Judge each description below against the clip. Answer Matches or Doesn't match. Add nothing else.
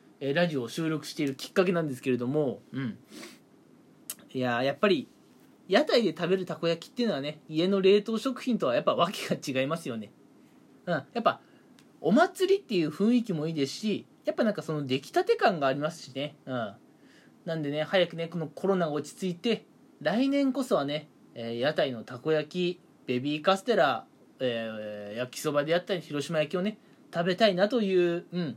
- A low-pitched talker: Doesn't match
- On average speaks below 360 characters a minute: Doesn't match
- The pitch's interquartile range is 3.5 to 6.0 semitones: Matches